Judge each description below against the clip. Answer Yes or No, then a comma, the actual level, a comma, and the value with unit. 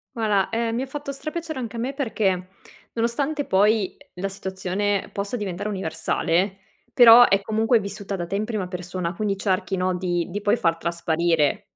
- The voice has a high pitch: Yes, high, 200 Hz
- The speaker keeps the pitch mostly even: No, average, 3.8 semitones